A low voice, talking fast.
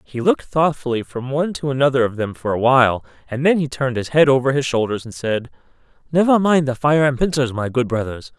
Yes: low, 130 Hz; fast, 230 wpm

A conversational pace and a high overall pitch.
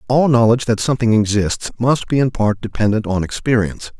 No: average, 180 wpm; low, 115 Hz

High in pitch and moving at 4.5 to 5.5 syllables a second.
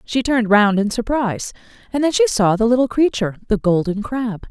No: high, 225 Hz; 5.7 syllables/s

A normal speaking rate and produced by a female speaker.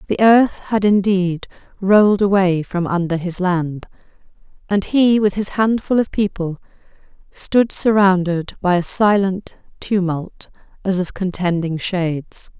No: slow, 130 wpm; female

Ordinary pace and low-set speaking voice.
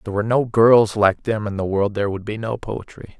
No: fast, 280 wpm; low, 105 Hz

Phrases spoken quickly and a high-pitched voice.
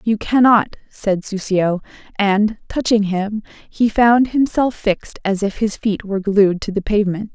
No: average, 165 wpm; high, 205 Hz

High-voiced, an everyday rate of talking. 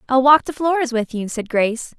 No: very high, 255 Hz; fast, 240 wpm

